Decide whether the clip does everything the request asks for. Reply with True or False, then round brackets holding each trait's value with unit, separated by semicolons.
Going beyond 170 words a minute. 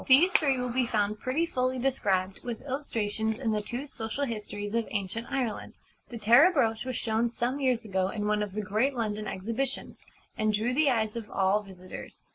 True (195 wpm)